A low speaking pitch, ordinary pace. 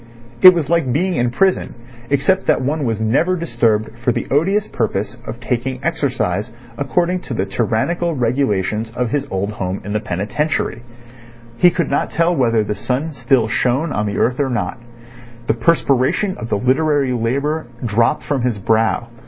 Yes: low, 125 Hz; average, 170 wpm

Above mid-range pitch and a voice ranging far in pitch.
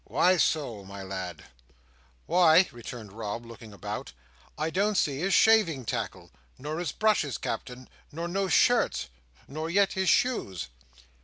No: medium, 150 Hz; wide, 8.6 semitones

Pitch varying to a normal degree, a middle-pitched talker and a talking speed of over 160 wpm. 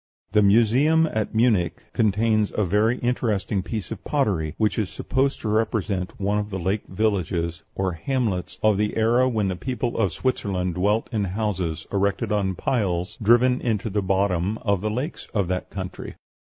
No: average, 3.1 semitones; low, 105 Hz; average, 170 wpm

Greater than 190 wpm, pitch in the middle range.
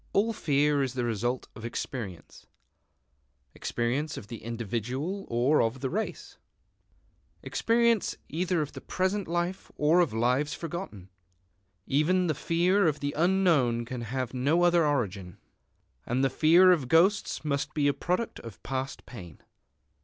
No: average, 145 wpm; medium, 145 Hz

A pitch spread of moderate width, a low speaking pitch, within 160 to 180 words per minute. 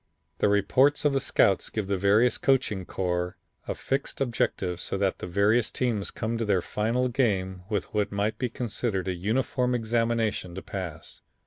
Yes: average, 4.2 semitones; low, 105 Hz; average, 175 wpm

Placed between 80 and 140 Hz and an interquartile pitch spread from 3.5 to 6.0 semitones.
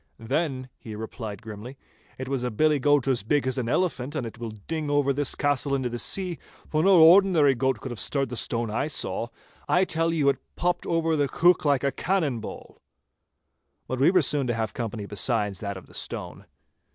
Yes: low, 135 Hz; average, 4.8 semitones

